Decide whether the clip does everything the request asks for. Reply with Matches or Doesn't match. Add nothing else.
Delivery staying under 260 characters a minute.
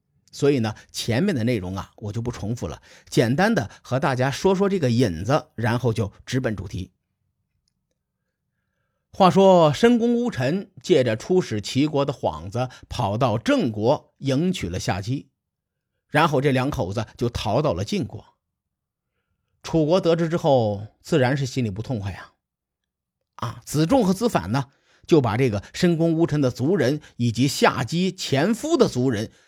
Matches